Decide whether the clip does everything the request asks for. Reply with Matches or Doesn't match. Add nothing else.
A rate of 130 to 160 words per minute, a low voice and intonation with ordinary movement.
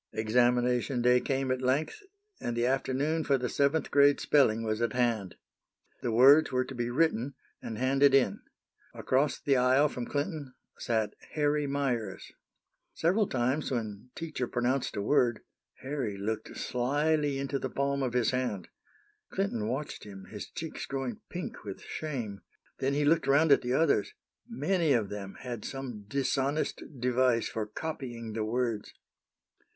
Matches